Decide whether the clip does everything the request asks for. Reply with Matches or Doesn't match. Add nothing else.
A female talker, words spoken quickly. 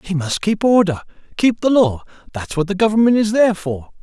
Doesn't match